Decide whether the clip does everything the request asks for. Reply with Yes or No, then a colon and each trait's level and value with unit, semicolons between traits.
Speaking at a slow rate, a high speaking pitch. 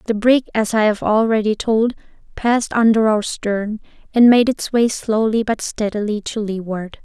No: average, 170 wpm; high, 220 Hz